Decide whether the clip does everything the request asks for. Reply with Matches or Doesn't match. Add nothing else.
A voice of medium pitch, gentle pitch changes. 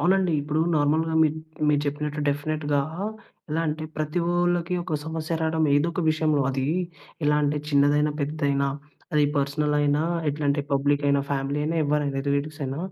Matches